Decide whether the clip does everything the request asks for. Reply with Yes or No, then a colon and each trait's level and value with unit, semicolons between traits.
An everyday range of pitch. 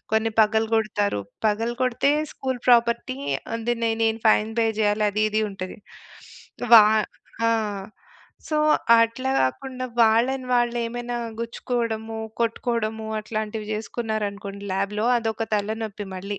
No: narrow, 1.9 semitones